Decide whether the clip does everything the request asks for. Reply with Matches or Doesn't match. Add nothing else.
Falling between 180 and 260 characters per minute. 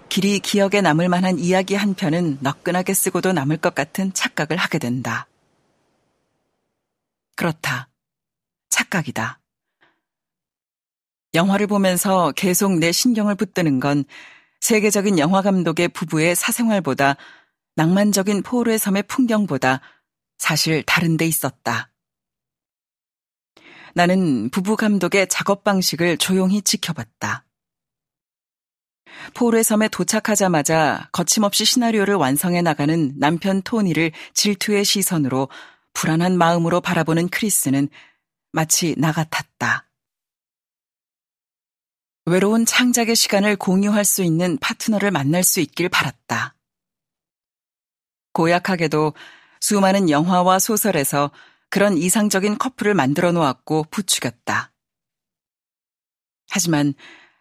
Matches